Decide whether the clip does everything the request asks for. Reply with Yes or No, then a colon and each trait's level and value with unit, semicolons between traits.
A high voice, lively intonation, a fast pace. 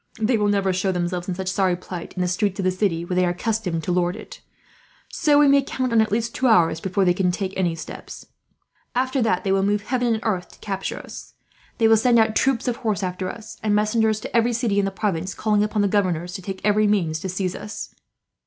No: high, 200 Hz; average, 3.4 semitones; fast, 245 wpm